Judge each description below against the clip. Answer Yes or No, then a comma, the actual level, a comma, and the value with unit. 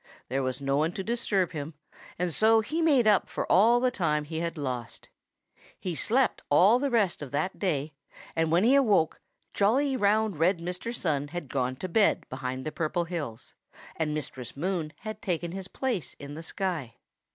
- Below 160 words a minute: No, average, 185 wpm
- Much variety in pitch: Yes, wide, 6.3 semitones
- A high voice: No, medium, 175 Hz